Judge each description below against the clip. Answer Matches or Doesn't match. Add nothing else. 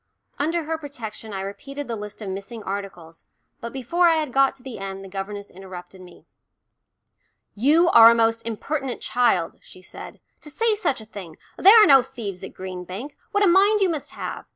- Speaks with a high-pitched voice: Matches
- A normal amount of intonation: Doesn't match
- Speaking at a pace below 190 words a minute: Doesn't match